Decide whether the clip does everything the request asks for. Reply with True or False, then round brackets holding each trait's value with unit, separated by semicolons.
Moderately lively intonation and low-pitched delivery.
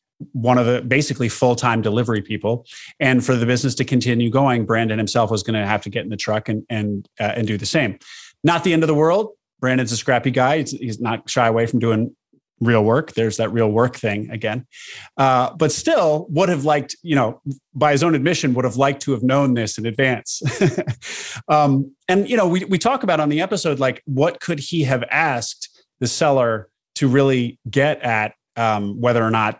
True (4.2 semitones; 125 Hz)